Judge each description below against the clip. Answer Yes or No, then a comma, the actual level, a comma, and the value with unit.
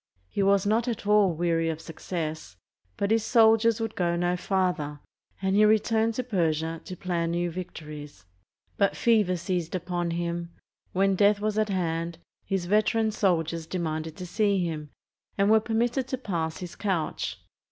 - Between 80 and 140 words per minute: No, average, 165 wpm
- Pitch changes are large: No, average, 4.1 semitones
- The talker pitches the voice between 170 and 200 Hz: Yes, medium, 185 Hz